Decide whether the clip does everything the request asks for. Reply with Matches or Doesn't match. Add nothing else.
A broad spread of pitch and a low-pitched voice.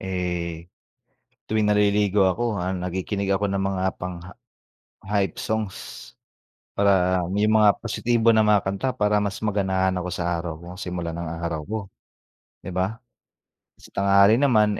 Doesn't match